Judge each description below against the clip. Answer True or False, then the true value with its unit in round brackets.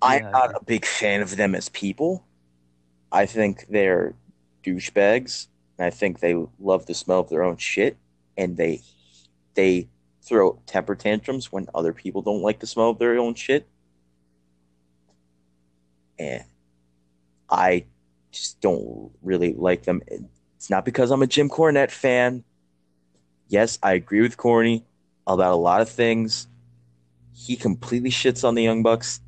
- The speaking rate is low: False (150 wpm)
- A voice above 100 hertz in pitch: False (90 Hz)